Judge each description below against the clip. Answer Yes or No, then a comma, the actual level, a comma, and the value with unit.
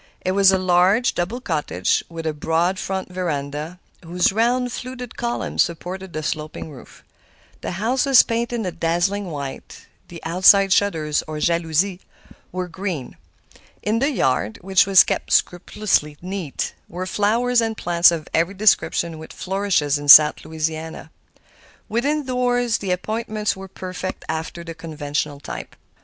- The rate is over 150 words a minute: No, average, 145 wpm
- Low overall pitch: No, medium, 180 Hz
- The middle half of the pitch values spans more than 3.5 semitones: Yes, average, 4.6 semitones